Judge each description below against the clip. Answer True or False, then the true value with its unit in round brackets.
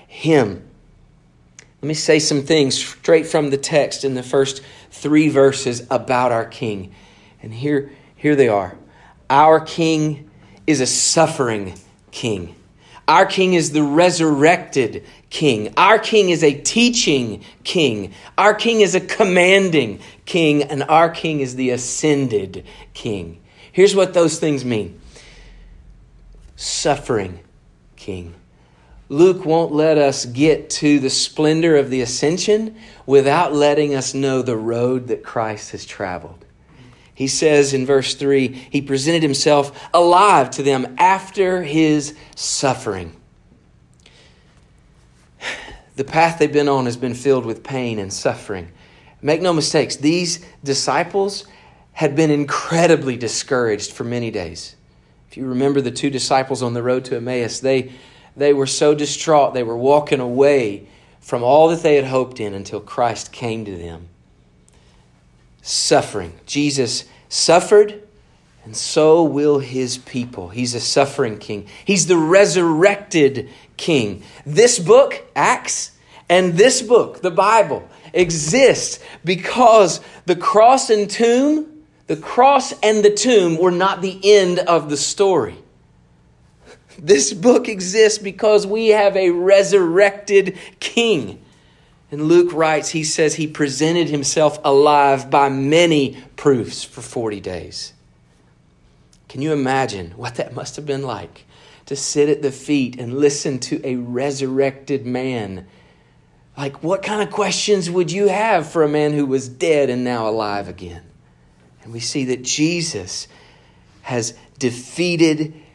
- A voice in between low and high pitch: True (145 Hz)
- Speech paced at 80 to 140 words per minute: True (135 wpm)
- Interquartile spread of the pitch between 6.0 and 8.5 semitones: False (5.5 semitones)